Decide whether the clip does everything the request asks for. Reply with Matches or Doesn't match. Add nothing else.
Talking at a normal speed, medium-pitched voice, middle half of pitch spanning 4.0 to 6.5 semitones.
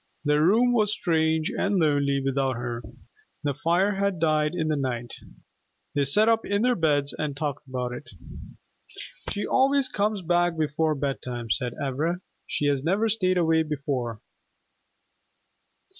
Matches